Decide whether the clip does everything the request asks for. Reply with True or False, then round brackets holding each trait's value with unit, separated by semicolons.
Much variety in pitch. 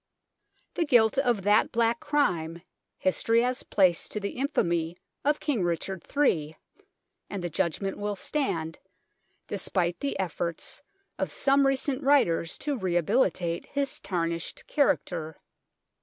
True (7.6 semitones)